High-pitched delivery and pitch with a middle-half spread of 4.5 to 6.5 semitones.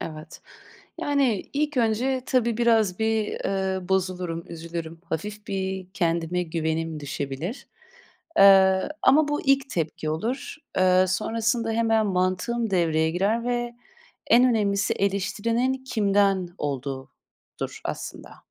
Yes: high, 195 Hz; average, 5.2 semitones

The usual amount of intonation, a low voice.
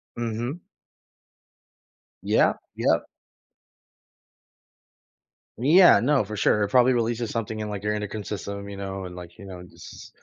Yes: average, 3.0 semitones; low, 105 Hz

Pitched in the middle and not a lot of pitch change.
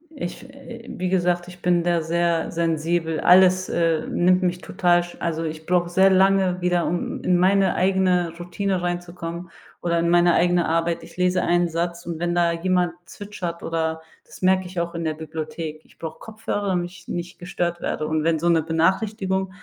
Yes: medium, 175 Hz; narrow, 1.6 semitones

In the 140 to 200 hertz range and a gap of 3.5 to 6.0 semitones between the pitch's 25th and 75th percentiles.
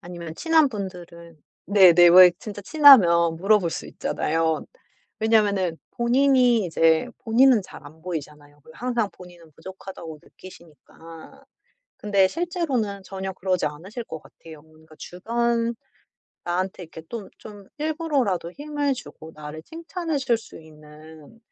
No: high, 190 Hz; wide, 6.5 semitones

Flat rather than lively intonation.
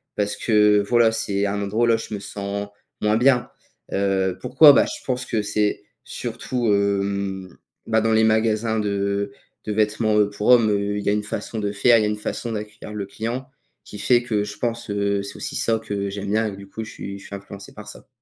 Yes: narrow, 1.8 semitones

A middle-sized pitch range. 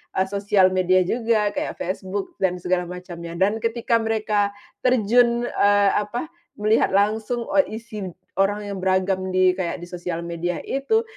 Yes: average, 3.2 semitones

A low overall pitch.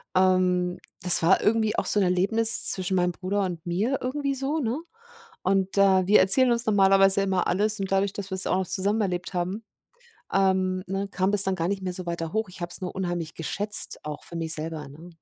No: high, 190 Hz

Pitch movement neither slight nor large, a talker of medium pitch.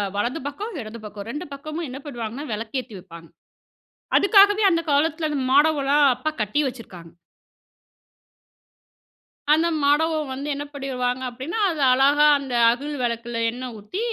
No: average, 4.4 semitones; very high, 270 Hz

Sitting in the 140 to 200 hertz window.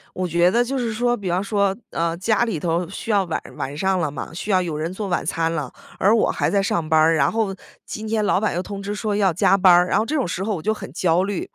Yes: high, 190 Hz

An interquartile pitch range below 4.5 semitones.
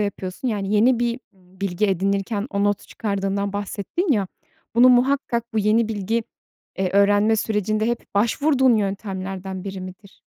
Yes: average, 2.9 semitones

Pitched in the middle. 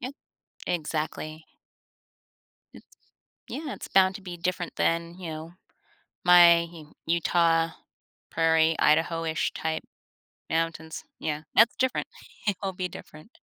Yes: medium, 165 Hz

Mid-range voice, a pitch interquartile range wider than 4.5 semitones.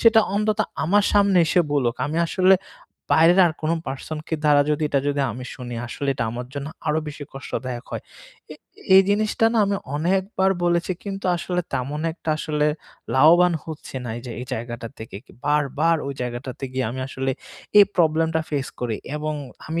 Yes: medium, 150 Hz; average, 5.1 semitones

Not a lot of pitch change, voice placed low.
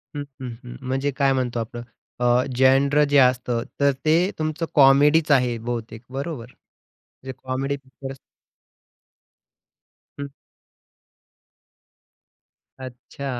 Yes: narrow, 2.3 semitones; low, 130 Hz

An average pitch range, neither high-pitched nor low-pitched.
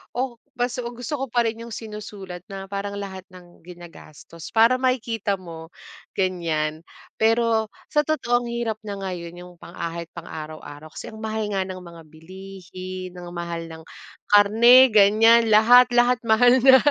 No: average, 5.0 semitones; high, 200 Hz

